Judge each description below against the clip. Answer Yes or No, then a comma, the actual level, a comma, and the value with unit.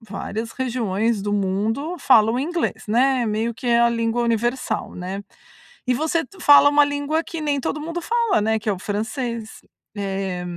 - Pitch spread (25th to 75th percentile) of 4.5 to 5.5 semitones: Yes, average, 5.2 semitones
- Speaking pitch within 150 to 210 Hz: No, high, 235 Hz